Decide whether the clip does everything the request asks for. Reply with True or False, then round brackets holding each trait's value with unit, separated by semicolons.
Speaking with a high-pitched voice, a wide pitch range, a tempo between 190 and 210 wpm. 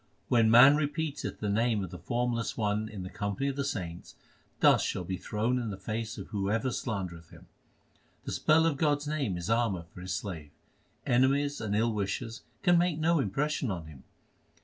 False (115 Hz; 6.1 semitones; 195 wpm)